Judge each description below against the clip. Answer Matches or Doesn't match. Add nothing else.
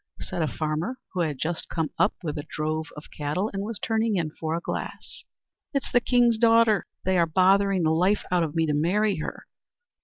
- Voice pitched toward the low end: Doesn't match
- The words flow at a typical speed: Doesn't match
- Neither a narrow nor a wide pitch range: Matches